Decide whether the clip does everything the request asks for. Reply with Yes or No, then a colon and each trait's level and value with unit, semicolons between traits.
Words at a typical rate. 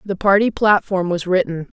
Yes: average, 170 wpm